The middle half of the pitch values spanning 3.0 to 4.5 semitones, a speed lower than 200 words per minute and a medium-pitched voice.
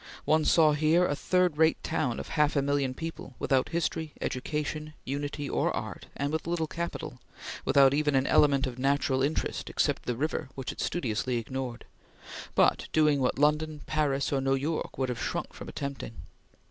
No: narrow, 2.6 semitones; average, 175 wpm; medium, 145 Hz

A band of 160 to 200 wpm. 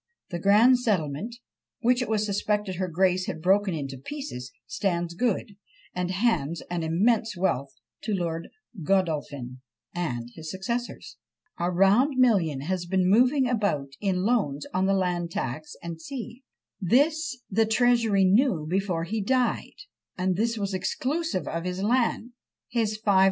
No: average, 145 wpm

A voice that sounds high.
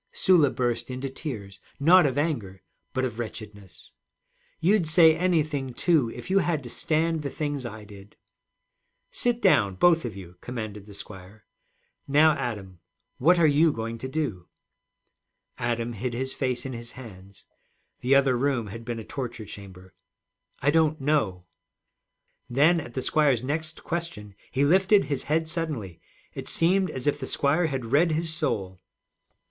No: low, 130 Hz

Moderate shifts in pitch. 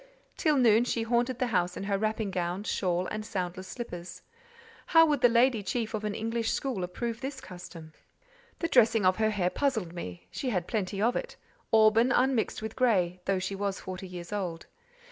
Yes: average, 4.6 semitones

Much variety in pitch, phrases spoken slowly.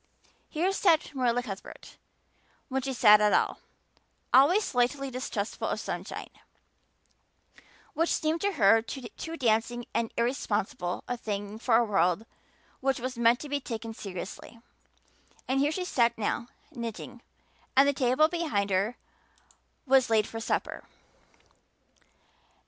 No: average, 3.8 semitones; slow, 130 wpm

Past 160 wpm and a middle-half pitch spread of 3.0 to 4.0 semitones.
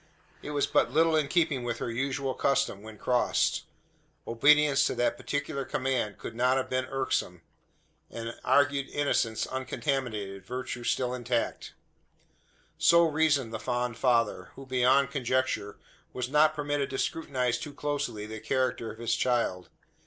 No: average, 145 wpm; average, 3.3 semitones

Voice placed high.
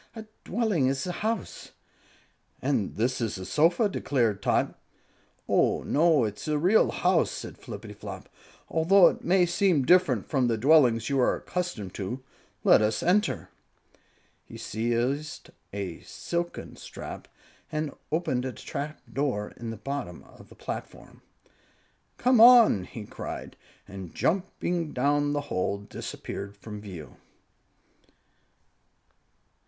No: medium, 140 Hz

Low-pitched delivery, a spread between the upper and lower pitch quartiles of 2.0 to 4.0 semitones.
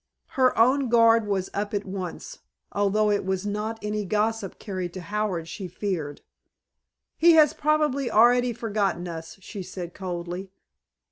No: high, 205 Hz; average, 3.5 semitones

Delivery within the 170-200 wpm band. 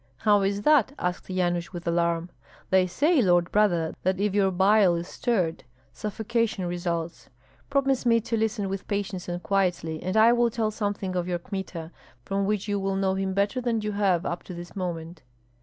Yes: average, 190 wpm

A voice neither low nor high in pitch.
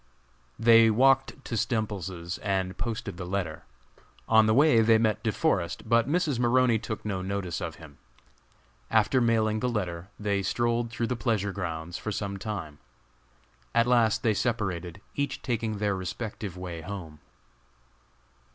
No: low, 110 Hz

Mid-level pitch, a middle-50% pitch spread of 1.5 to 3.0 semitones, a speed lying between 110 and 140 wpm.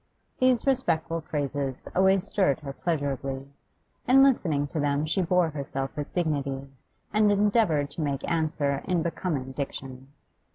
No: medium, 155 Hz; average, 4.6 semitones; slow, 135 wpm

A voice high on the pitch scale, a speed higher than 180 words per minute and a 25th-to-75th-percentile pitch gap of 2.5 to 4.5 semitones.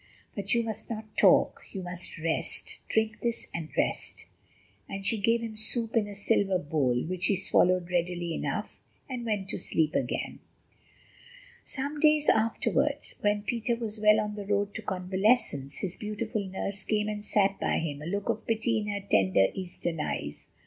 No: high, 205 Hz; average, 175 wpm; average, 3.5 semitones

